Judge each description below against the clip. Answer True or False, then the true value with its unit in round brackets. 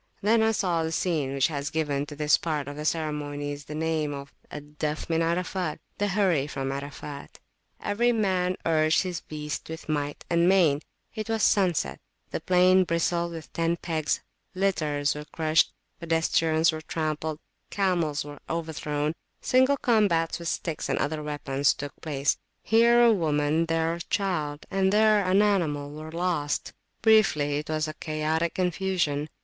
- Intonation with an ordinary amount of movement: True (3.5 semitones)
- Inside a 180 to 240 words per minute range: False (160 wpm)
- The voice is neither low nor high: True (160 Hz)